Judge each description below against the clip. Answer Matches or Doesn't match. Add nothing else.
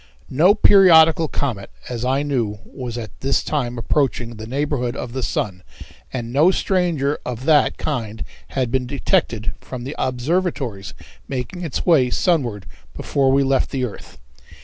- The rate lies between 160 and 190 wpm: Doesn't match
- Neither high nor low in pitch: Doesn't match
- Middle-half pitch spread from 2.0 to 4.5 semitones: Matches